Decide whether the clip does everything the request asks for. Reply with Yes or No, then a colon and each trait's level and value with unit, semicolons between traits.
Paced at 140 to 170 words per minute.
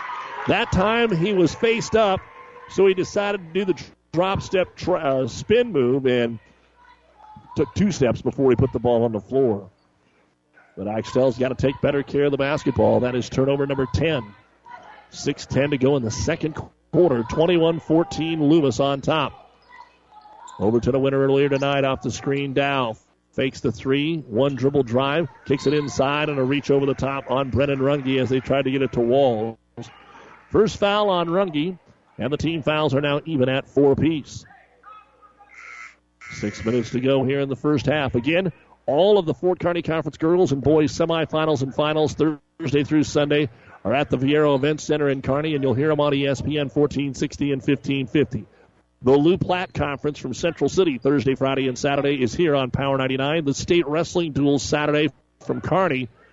No: average, 185 wpm